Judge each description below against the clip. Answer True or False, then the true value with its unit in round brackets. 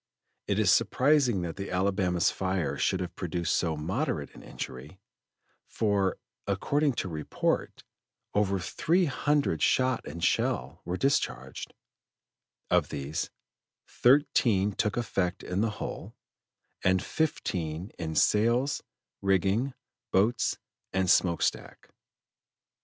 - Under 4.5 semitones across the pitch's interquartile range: False (5.6 semitones)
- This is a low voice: True (95 Hz)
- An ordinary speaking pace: False (115 wpm)